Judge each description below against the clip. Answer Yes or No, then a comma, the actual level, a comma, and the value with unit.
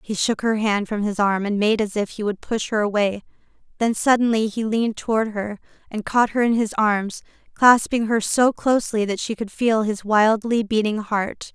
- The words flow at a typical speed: No, fast, 210 wpm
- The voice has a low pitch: No, high, 215 Hz